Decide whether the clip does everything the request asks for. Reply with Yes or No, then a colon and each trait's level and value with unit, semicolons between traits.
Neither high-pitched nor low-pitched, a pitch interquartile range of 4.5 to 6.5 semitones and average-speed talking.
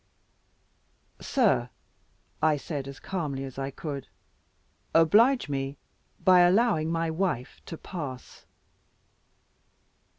No: medium, 155 Hz; average, 5.1 semitones; slow, 95 wpm